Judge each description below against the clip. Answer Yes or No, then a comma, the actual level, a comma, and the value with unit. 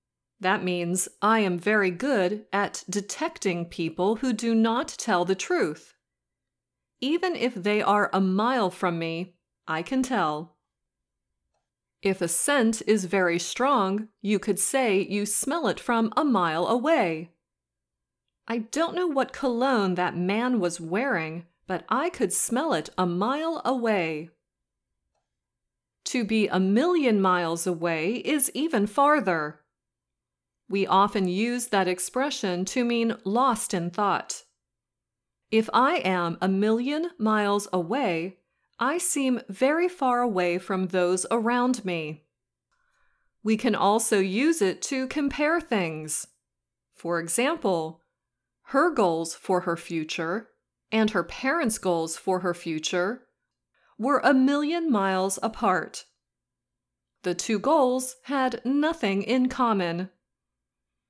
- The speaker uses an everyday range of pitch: No, wide, 6.0 semitones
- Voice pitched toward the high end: Yes, high, 205 Hz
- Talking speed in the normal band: No, slow, 125 wpm